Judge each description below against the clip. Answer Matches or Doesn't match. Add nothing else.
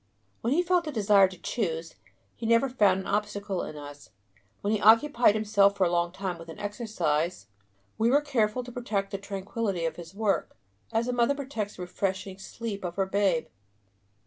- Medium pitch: Doesn't match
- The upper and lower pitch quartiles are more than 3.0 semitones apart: Matches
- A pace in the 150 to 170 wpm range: Doesn't match